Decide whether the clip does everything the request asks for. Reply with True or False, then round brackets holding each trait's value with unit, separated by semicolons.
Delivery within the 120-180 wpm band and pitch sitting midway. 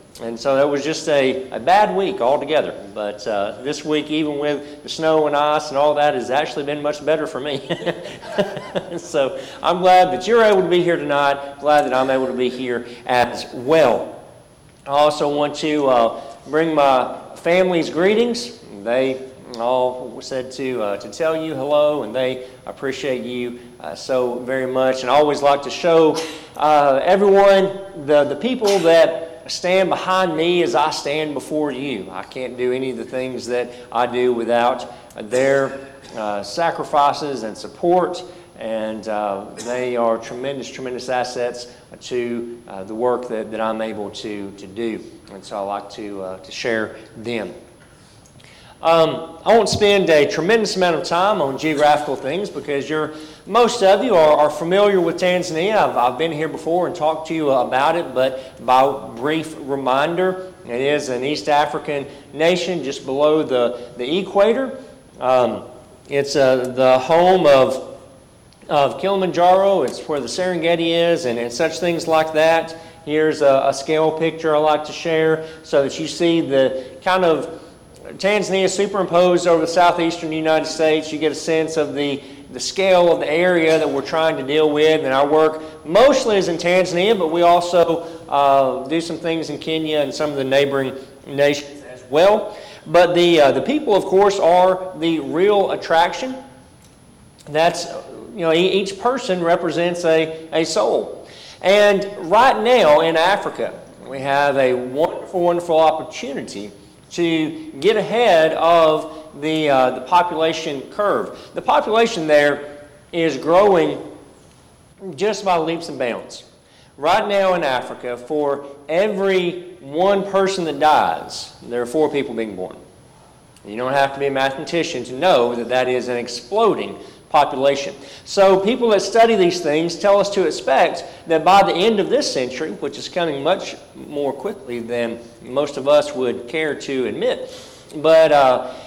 True (165 wpm; 150 Hz)